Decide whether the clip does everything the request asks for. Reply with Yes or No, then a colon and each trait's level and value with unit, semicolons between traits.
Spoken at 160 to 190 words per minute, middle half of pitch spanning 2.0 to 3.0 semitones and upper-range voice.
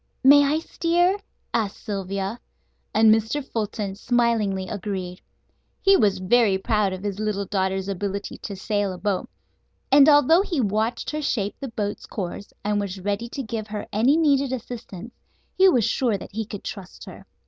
No: average, 170 wpm; average, 4.1 semitones; high, 215 Hz